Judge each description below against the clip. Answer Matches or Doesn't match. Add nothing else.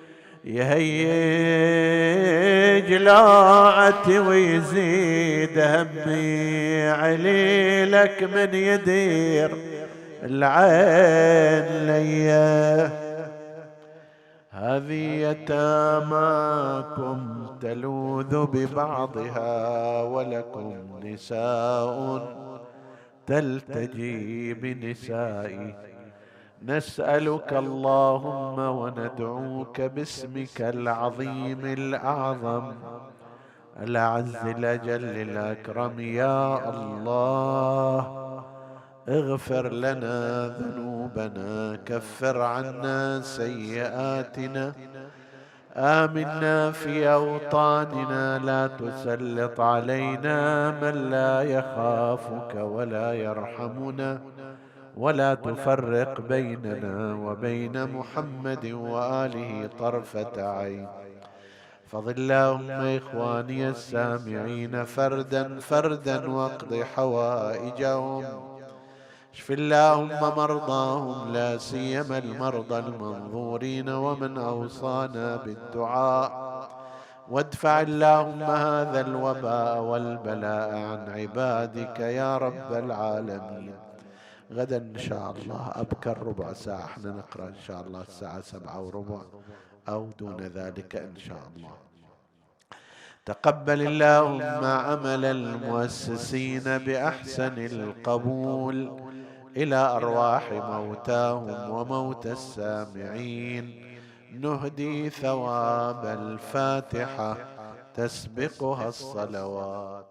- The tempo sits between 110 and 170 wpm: Doesn't match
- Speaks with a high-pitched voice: Doesn't match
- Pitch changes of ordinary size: Matches